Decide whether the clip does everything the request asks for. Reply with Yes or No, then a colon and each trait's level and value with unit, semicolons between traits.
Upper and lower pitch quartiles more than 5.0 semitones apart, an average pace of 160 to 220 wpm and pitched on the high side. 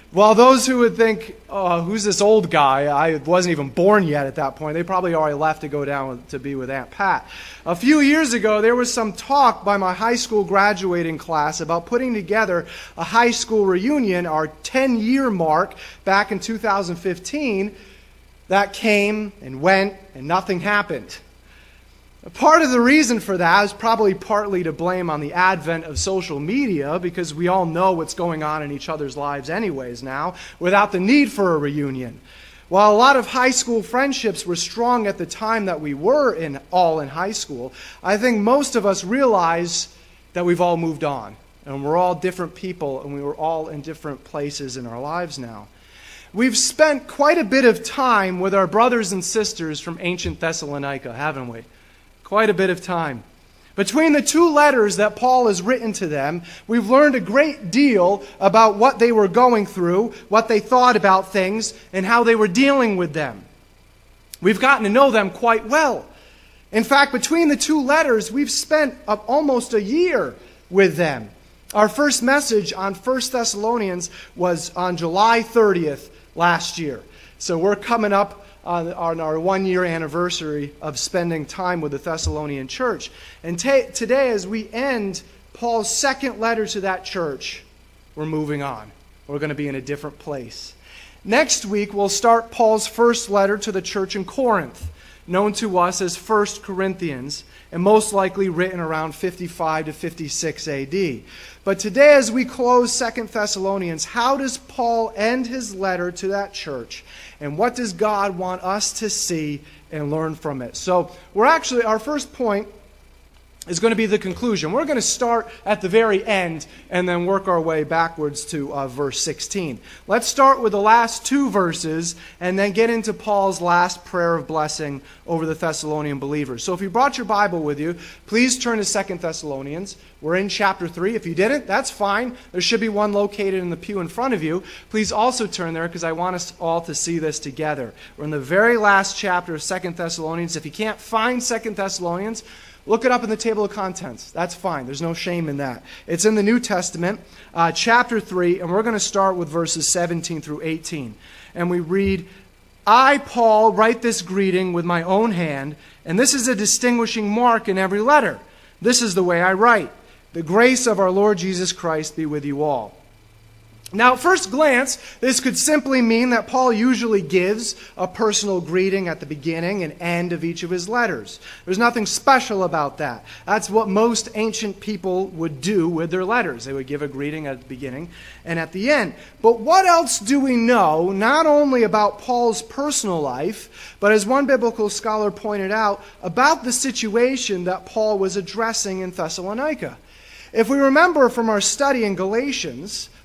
Yes: wide, 5.6 semitones; average, 185 wpm; high, 195 Hz